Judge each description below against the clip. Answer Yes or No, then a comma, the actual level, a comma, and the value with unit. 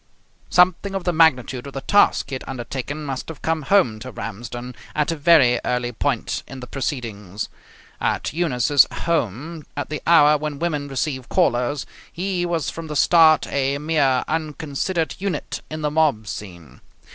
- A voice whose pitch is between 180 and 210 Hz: No, medium, 145 Hz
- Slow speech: No, average, 165 wpm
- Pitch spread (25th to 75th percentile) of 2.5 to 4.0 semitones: No, average, 4.4 semitones